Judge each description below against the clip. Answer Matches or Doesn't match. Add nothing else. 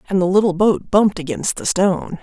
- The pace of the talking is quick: Matches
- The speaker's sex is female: Matches